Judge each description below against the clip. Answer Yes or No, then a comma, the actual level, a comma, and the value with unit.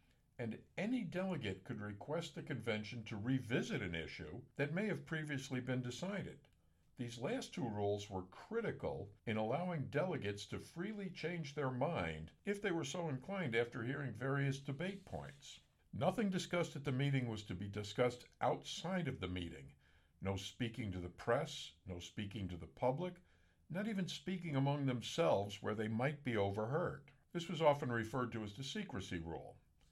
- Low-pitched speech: Yes, low, 125 Hz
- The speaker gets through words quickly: No, average, 165 wpm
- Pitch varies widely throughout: Yes, wide, 8.0 semitones